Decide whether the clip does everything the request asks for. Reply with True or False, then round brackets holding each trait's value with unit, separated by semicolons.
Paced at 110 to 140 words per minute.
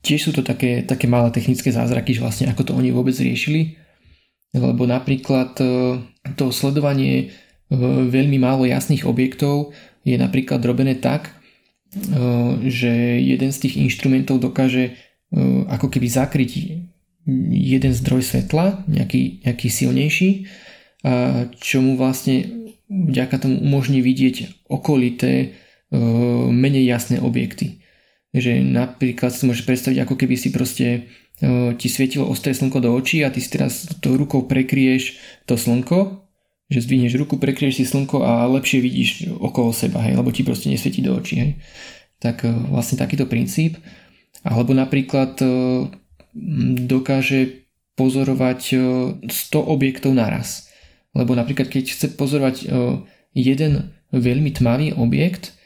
True (130 wpm)